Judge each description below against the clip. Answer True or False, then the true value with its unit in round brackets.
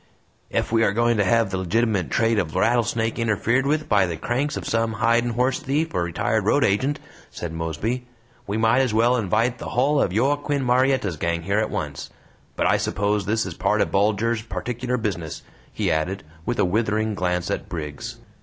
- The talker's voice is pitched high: False (110 Hz)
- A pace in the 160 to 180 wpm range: False (190 wpm)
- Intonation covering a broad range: False (4.0 semitones)